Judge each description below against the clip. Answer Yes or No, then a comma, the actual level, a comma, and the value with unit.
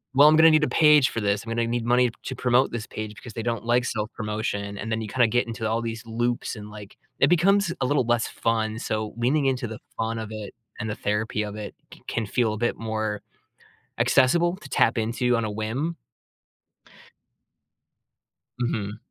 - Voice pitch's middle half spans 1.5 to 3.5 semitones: Yes, narrow, 2.5 semitones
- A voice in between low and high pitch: No, low, 115 Hz